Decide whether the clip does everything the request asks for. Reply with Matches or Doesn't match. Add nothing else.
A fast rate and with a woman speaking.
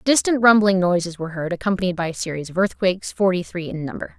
Matches